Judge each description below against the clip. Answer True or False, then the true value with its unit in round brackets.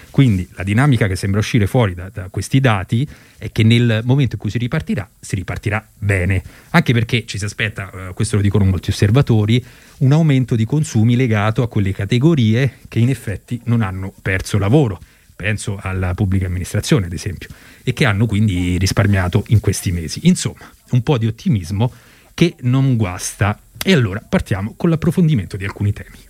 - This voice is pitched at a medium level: False (110 Hz)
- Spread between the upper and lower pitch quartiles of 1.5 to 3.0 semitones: False (4.0 semitones)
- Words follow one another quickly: True (180 wpm)